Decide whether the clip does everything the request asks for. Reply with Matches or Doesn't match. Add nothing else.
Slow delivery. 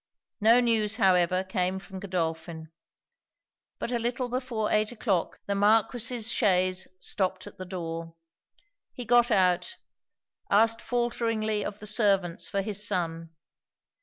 Matches